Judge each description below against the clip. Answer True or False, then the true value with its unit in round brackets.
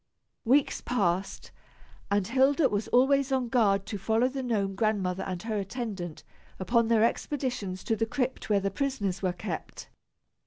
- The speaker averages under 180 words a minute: True (155 wpm)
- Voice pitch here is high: True (220 Hz)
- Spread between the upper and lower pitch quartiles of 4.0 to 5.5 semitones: True (4.4 semitones)